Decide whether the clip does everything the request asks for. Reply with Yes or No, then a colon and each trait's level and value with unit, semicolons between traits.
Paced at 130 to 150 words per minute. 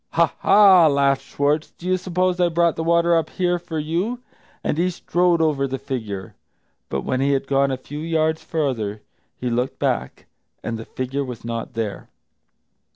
No: average, 180 wpm